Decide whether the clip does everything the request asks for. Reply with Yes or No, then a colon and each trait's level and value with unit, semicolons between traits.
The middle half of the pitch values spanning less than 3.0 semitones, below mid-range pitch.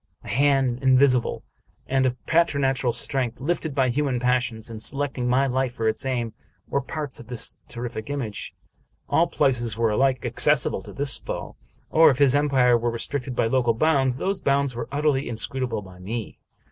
Yes: narrow, 2.6 semitones; low, 130 Hz